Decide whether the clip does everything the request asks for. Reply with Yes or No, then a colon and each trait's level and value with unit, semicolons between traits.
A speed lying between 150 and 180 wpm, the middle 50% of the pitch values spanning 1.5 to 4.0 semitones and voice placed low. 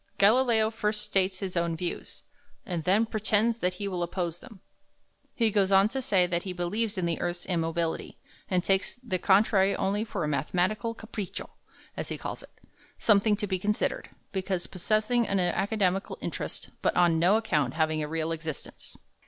No: average, 175 wpm; average, 3.5 semitones; high, 190 Hz